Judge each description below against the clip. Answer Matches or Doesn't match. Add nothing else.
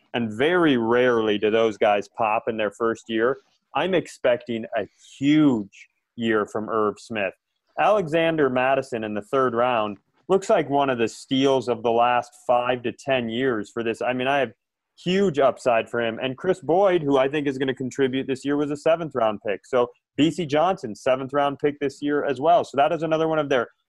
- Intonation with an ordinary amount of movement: Matches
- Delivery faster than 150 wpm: Matches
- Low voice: Matches